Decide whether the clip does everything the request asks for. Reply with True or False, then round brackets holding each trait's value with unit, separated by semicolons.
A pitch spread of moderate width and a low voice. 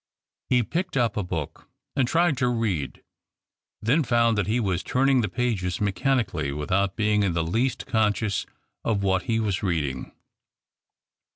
True (4.8 semitones; 105 Hz)